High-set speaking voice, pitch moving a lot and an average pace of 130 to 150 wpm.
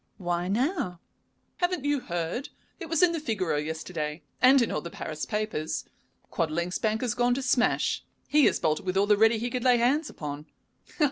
No: high, 215 Hz; wide, 7.2 semitones; average, 190 wpm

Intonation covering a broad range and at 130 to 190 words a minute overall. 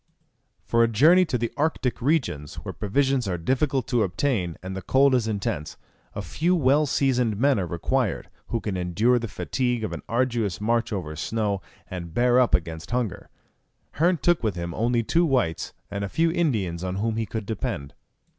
Yes: wide, 5.7 semitones; average, 185 wpm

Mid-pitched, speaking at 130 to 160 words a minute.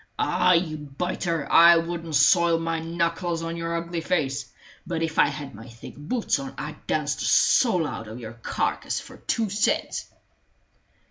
No: medium, 165 Hz; average, 170 wpm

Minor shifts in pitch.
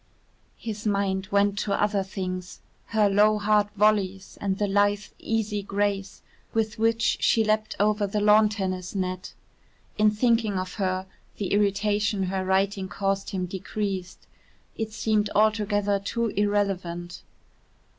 Yes: narrow, 1.7 semitones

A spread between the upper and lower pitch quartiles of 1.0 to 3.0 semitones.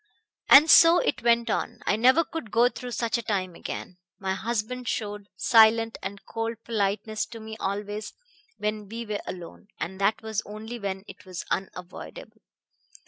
Yes: average, 2.7 semitones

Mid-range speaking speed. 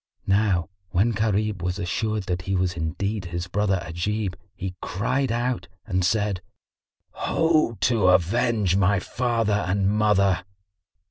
No: slow, 130 wpm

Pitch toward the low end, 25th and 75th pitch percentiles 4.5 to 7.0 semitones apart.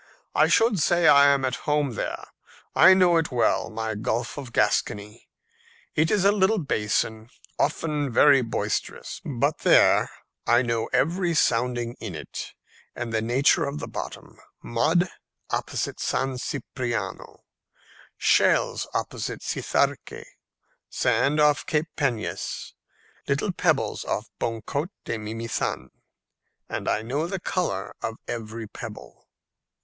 Yes: low, 130 Hz; average, 5.2 semitones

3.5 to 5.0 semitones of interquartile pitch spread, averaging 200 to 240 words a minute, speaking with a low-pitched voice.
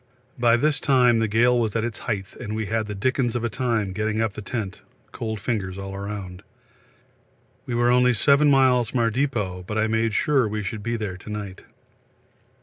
No: average, 2.7 semitones; fast, 205 wpm; low, 110 Hz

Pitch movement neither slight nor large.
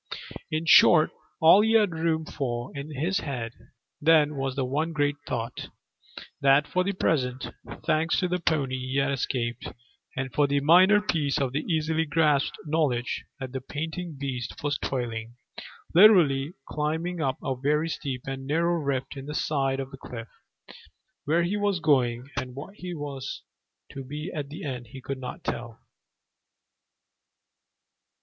Yes: average, 3.5 semitones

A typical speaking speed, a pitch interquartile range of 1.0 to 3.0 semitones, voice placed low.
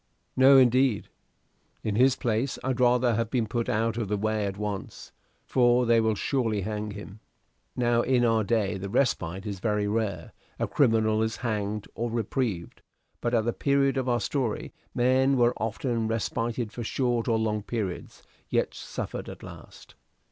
Yes: average, 170 wpm; narrow, 2.6 semitones; low, 115 Hz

